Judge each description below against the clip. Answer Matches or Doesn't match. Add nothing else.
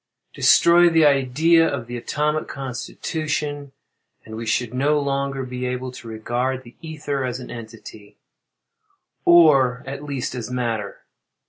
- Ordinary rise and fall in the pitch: Matches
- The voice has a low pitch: Matches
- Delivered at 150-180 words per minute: Doesn't match